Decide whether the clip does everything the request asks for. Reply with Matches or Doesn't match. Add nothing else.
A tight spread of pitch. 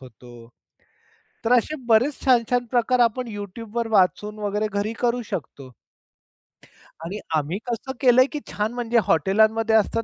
Doesn't match